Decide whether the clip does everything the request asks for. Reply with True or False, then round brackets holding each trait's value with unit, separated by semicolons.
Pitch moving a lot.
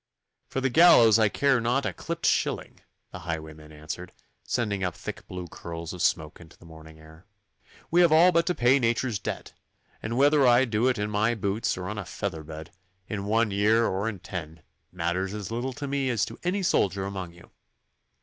True (6.5 semitones)